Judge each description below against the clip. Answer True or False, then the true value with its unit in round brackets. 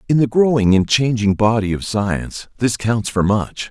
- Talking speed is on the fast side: False (195 wpm)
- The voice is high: False (110 Hz)